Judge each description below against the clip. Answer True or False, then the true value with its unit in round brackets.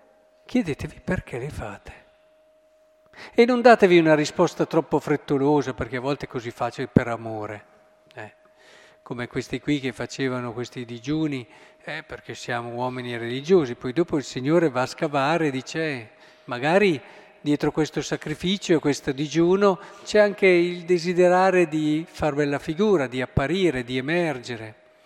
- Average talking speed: True (145 wpm)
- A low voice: False (150 Hz)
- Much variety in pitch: True (5.7 semitones)